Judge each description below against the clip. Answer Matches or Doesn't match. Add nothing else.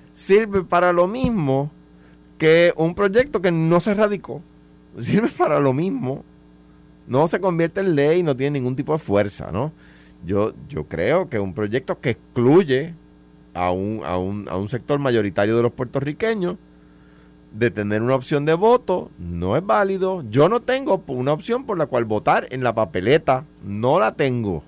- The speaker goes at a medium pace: Matches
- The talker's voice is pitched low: Matches